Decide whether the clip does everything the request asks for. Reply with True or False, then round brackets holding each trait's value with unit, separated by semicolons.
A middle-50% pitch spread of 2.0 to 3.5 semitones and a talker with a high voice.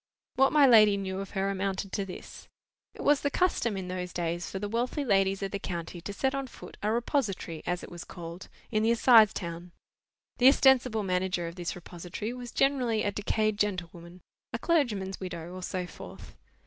False (4.5 semitones; 195 Hz)